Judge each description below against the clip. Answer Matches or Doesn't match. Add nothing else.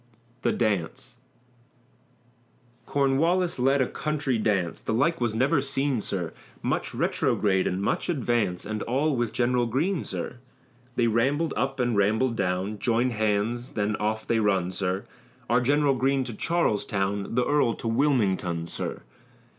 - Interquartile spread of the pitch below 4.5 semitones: Doesn't match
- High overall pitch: Doesn't match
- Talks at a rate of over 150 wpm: Doesn't match